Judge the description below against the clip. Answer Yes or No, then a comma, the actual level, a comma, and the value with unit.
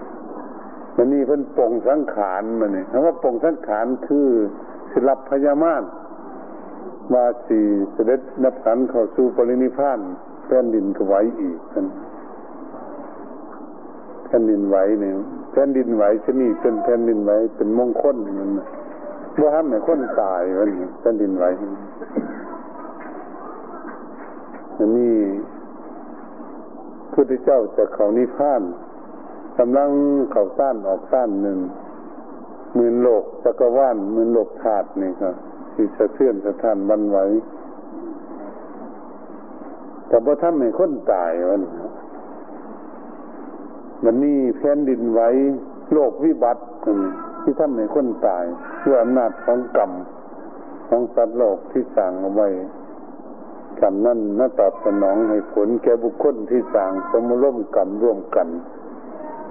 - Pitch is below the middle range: No, medium, 145 Hz